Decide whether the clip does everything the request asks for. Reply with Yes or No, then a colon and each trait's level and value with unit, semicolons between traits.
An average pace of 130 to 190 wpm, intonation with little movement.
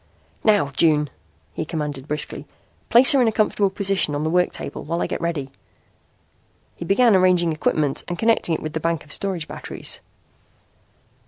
No: average, 170 wpm; average, 4.5 semitones